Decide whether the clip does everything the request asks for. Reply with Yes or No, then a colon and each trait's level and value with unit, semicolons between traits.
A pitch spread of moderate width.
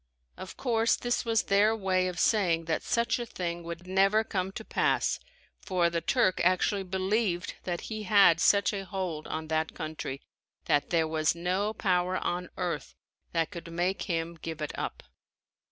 Yes: average, 3.2 semitones